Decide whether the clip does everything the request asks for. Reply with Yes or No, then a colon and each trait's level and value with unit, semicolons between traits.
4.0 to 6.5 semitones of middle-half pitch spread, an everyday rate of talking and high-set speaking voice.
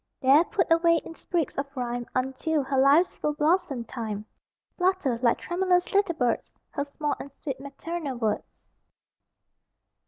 Yes: average, 4.7 semitones; average, 145 wpm; very high, 285 Hz